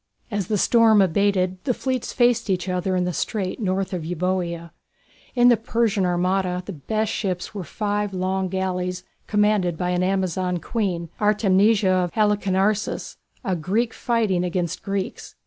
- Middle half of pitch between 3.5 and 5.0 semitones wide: No, narrow, 2.5 semitones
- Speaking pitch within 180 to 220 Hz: Yes, high, 190 Hz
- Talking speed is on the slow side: No, average, 150 wpm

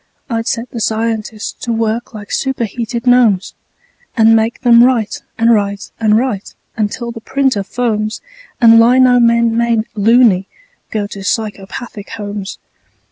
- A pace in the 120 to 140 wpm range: Yes, slow, 135 wpm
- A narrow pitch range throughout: Yes, narrow, 2.0 semitones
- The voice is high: Yes, high, 225 Hz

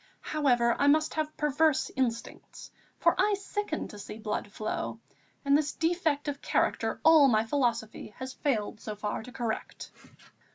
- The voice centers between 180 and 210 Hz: No, very high, 270 Hz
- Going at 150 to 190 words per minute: Yes, average, 155 wpm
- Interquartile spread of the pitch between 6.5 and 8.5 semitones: No, wide, 5.5 semitones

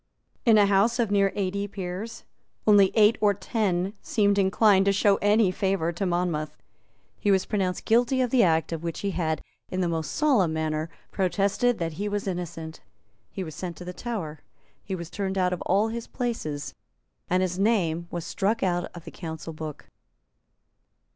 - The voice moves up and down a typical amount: Yes, average, 3.3 semitones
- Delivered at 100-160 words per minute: No, average, 180 wpm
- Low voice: No, high, 190 Hz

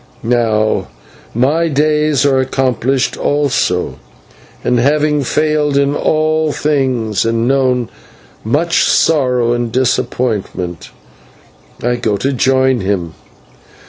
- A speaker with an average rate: No, slow, 100 wpm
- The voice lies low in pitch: Yes, low, 130 Hz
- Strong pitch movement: No, average, 3.7 semitones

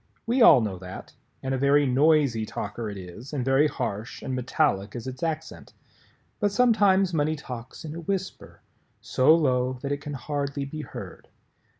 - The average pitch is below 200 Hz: Yes, medium, 140 Hz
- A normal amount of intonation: Yes, average, 4.0 semitones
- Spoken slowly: No, average, 175 wpm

